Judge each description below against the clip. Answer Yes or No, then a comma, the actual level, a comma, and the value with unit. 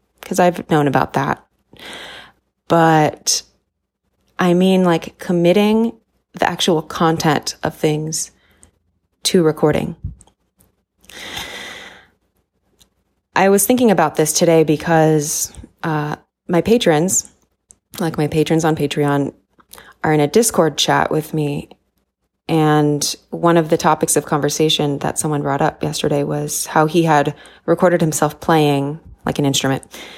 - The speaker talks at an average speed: No, slow, 120 wpm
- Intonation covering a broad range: No, narrow, 2.4 semitones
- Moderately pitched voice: Yes, medium, 155 Hz